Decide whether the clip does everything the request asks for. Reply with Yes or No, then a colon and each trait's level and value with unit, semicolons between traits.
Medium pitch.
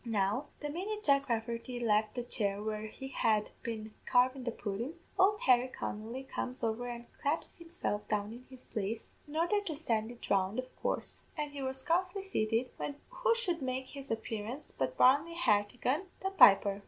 No: very high, 250 Hz